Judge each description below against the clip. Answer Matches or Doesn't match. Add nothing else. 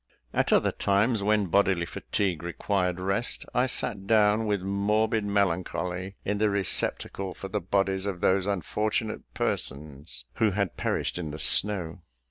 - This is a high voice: Doesn't match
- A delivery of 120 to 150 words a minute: Matches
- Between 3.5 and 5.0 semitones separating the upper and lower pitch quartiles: Doesn't match